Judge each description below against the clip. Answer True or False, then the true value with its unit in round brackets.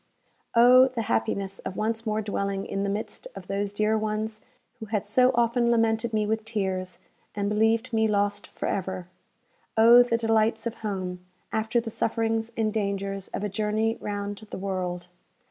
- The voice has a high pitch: True (215 Hz)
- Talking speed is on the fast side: False (170 wpm)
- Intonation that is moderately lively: False (2.2 semitones)